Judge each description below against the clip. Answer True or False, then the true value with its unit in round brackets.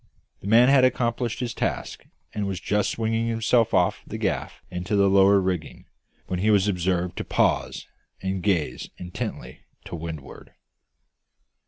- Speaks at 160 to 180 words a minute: False (150 wpm)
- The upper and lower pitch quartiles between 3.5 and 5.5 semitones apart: True (3.9 semitones)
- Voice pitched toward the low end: True (100 Hz)